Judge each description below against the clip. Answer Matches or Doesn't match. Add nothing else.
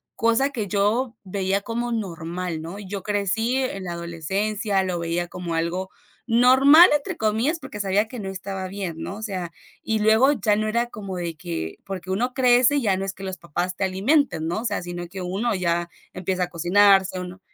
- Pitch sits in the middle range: Doesn't match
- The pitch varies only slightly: Doesn't match